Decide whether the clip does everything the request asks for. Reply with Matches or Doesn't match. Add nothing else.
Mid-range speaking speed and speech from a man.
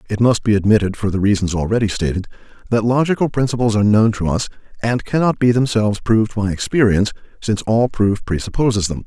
Matches